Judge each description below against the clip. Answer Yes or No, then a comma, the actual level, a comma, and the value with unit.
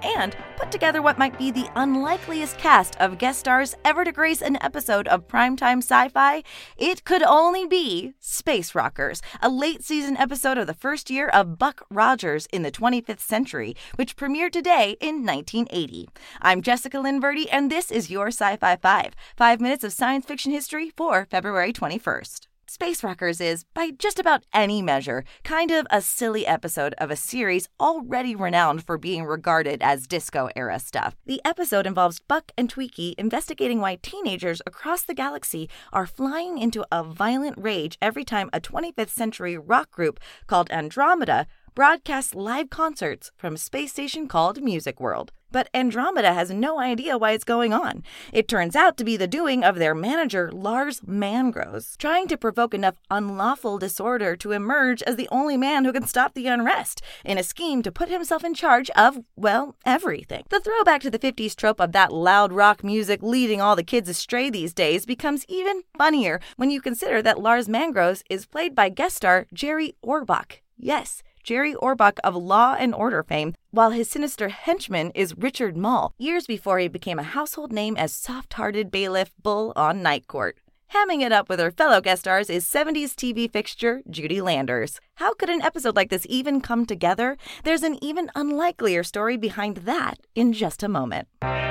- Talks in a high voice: Yes, high, 240 Hz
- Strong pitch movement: Yes, wide, 6.8 semitones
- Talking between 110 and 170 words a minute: No, average, 180 wpm